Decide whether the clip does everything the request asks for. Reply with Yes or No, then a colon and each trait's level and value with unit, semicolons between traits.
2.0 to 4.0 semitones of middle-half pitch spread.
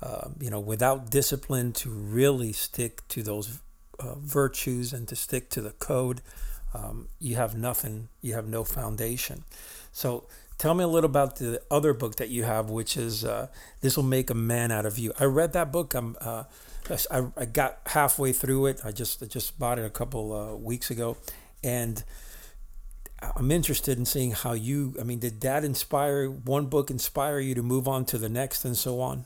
Yes: average, 3.0 semitones